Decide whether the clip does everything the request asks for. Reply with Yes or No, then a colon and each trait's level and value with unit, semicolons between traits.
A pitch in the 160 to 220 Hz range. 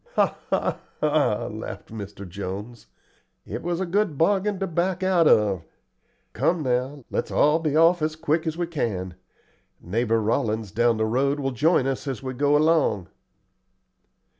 No: medium, 140 Hz